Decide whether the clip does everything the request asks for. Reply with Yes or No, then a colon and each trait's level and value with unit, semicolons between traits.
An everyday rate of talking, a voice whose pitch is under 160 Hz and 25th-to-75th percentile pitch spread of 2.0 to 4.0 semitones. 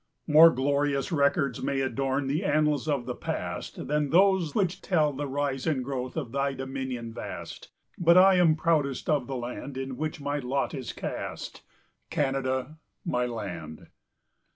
Yes: average, 155 wpm; medium, 140 Hz; average, 2.7 semitones